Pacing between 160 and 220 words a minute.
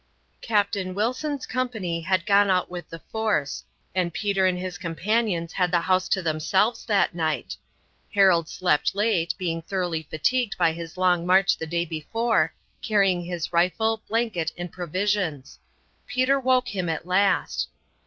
No: average, 150 wpm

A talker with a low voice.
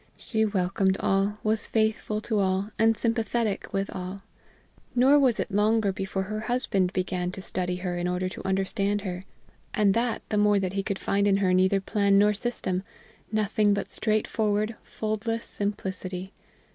No: high, 200 Hz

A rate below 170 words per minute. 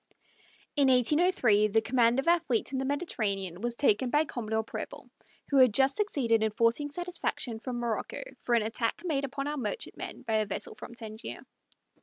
No: average, 180 wpm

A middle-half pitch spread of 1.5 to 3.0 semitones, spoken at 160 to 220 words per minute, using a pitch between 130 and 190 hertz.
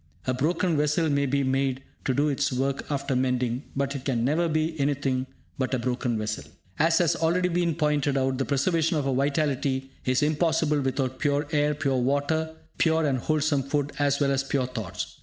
Yes: narrow, 2.5 semitones; average, 195 wpm; medium, 140 Hz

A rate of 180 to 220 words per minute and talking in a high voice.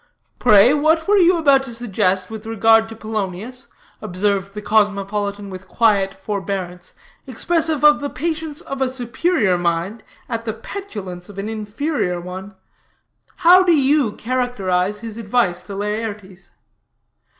No: average, 140 wpm; high, 220 Hz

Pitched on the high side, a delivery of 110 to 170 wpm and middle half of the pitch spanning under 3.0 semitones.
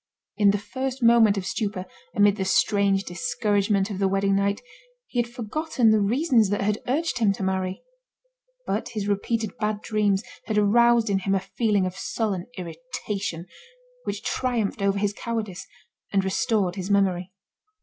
Yes: high, 205 Hz; average, 160 wpm; narrow, 2.6 semitones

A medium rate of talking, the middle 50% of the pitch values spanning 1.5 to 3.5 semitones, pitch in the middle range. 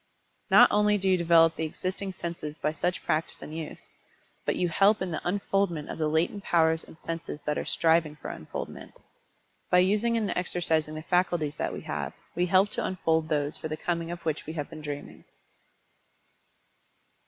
Yes: average, 185 wpm; average, 2.7 semitones; medium, 165 Hz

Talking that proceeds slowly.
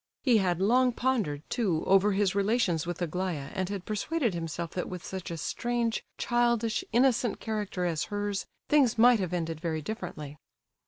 No: average, 165 wpm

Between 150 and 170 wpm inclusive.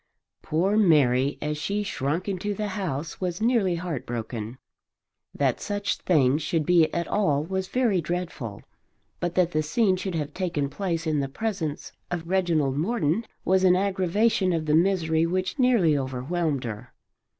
Yes: average, 155 wpm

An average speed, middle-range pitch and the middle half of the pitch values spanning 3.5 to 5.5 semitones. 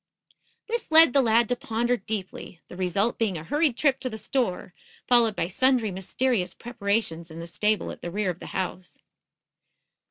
No: average, 180 wpm; high, 220 Hz; average, 5.1 semitones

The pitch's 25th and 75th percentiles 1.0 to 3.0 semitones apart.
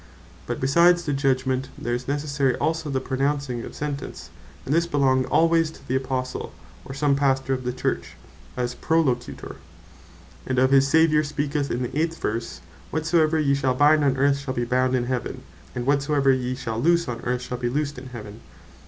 Yes: narrow, 2.6 semitones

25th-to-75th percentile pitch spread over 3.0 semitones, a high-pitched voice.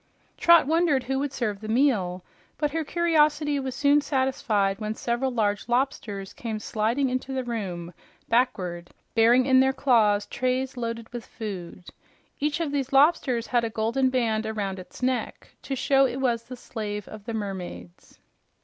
Yes: average, 4.0 semitones; high, 240 Hz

